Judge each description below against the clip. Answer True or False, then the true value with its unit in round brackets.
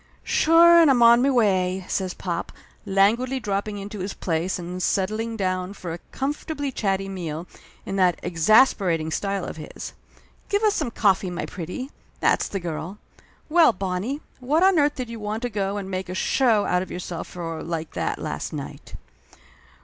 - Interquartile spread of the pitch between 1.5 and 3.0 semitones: False (5.3 semitones)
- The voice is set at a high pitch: True (195 Hz)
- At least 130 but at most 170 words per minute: False (180 wpm)